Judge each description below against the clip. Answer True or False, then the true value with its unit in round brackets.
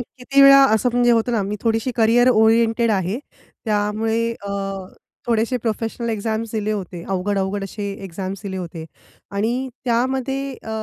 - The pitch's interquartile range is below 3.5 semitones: True (3.0 semitones)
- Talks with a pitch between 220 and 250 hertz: True (225 Hz)